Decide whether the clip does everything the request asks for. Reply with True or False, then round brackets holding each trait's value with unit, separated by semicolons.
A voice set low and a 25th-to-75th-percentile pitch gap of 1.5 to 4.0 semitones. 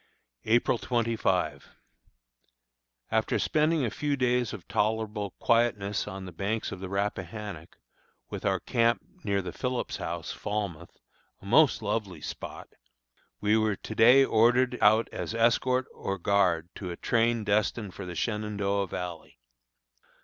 True (105 Hz; 3.1 semitones)